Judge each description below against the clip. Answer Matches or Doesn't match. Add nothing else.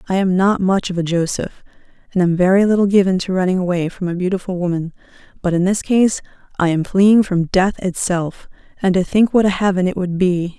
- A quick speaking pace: Matches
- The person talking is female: Matches